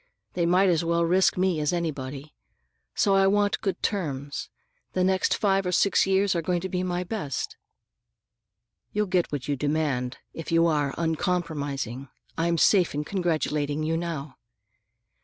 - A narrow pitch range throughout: No, average, 3.9 semitones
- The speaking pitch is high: No, medium, 170 Hz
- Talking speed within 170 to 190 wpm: No, average, 160 wpm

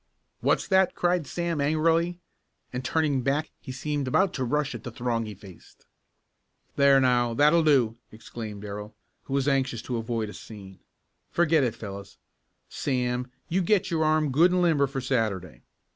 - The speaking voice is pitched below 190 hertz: Yes, low, 135 Hz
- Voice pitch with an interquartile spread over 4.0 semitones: Yes, average, 5.3 semitones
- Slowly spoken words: No, average, 165 wpm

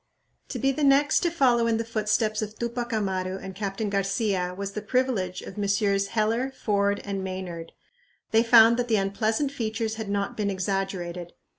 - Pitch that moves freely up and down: No, average, 3.0 semitones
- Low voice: No, high, 210 Hz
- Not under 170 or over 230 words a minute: Yes, average, 175 wpm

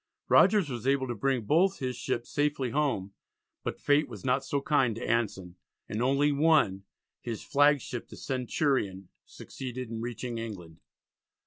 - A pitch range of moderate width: Yes, average, 4.0 semitones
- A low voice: Yes, low, 125 Hz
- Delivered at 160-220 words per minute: No, average, 150 wpm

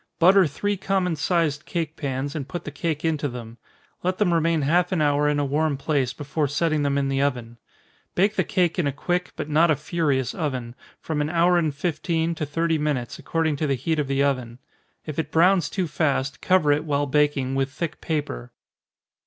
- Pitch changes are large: No, average, 3.2 semitones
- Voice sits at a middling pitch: Yes, medium, 150 Hz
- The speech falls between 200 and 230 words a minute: Yes, fast, 205 wpm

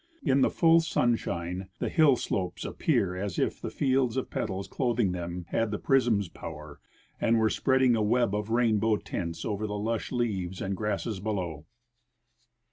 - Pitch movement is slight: No, average, 4.5 semitones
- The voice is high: No, low, 105 Hz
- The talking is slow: No, average, 165 wpm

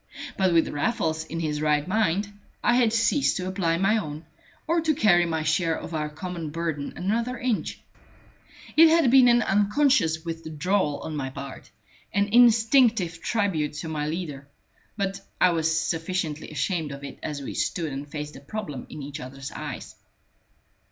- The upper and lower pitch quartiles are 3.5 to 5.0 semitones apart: No, wide, 5.5 semitones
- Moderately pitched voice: Yes, medium, 165 Hz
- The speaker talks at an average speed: Yes, average, 165 wpm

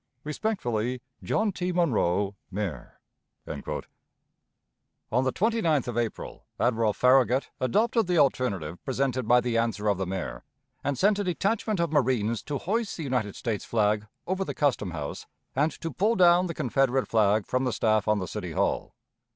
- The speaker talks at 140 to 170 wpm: Yes, average, 160 wpm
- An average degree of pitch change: No, wide, 8.0 semitones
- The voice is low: Yes, low, 125 Hz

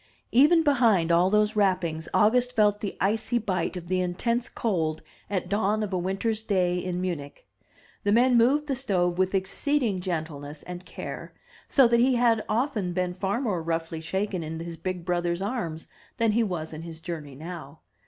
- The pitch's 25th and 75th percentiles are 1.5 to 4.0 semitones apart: No, average, 4.7 semitones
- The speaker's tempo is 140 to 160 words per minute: No, average, 180 wpm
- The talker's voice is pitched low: No, medium, 185 Hz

